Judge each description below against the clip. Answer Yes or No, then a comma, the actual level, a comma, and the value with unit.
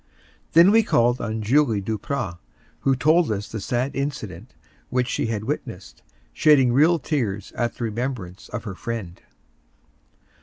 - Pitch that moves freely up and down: No, average, 4.7 semitones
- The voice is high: No, low, 120 Hz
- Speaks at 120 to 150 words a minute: Yes, average, 145 wpm